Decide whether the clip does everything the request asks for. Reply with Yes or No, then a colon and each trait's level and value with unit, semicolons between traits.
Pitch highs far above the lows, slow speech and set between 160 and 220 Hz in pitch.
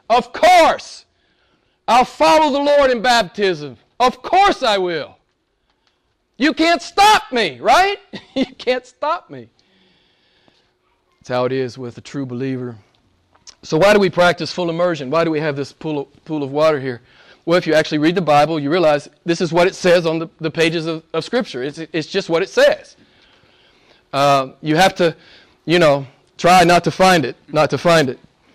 No: wide, 8.5 semitones; average, 175 wpm; medium, 170 Hz